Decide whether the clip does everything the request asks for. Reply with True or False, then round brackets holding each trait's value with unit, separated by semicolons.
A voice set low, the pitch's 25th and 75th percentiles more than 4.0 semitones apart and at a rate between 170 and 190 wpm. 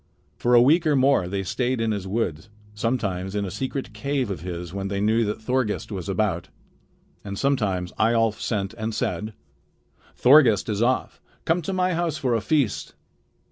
True (110 Hz; 4.8 semitones; 180 wpm)